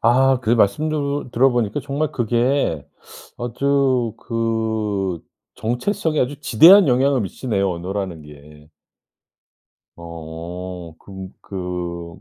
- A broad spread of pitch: Yes, wide, 6.8 semitones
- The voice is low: Yes, low, 110 Hz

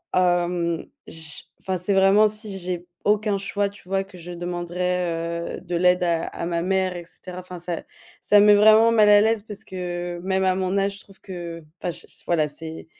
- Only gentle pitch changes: Yes, narrow, 2.3 semitones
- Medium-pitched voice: Yes, medium, 180 Hz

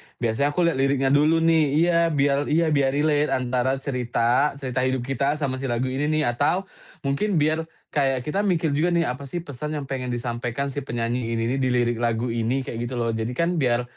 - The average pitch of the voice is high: No, low, 135 Hz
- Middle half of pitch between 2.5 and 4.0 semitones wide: Yes, average, 3.7 semitones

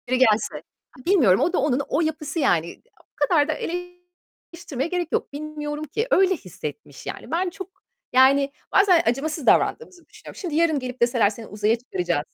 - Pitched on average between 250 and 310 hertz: Yes, very high, 300 Hz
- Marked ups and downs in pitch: Yes, wide, 6.0 semitones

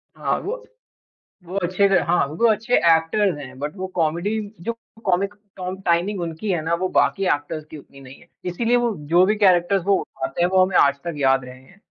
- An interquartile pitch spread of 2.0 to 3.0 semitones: No, average, 3.9 semitones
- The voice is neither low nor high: Yes, medium, 175 Hz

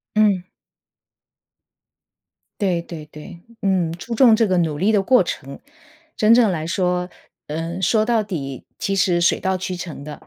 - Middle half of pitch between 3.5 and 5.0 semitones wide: Yes, average, 3.8 semitones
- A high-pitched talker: No, medium, 180 Hz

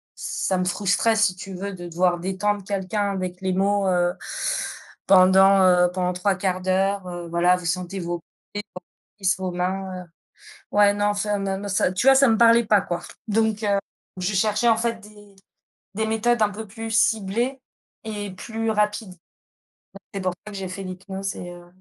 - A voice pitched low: No, high, 195 Hz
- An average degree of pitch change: No, narrow, 2.3 semitones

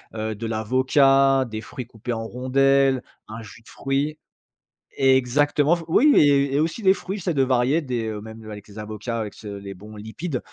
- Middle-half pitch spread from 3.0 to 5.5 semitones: Yes, average, 4.1 semitones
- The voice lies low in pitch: Yes, low, 130 Hz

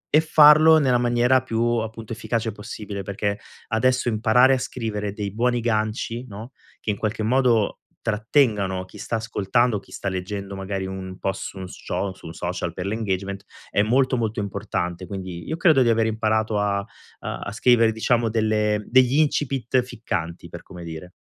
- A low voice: Yes, low, 110 Hz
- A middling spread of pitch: Yes, average, 3.5 semitones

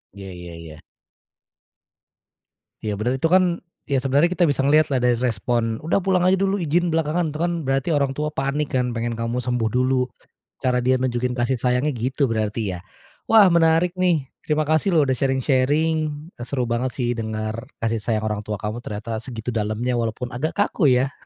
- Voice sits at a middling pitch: No, low, 130 Hz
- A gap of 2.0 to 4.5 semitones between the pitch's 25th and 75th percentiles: No, average, 4.9 semitones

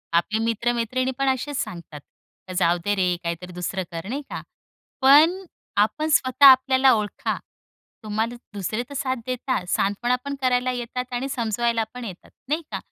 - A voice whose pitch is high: Yes, high, 240 Hz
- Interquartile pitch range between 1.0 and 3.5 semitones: No, average, 4.2 semitones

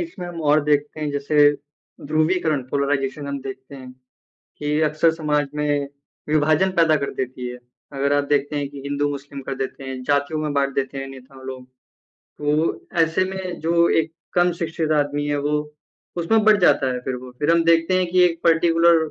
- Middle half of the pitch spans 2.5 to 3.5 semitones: Yes, average, 2.8 semitones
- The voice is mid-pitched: Yes, medium, 150 Hz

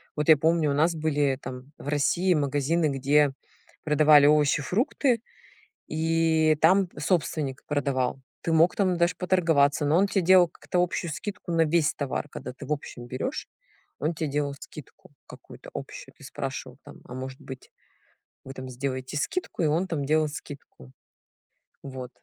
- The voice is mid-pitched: Yes, medium, 150 Hz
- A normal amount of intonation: Yes, average, 3.3 semitones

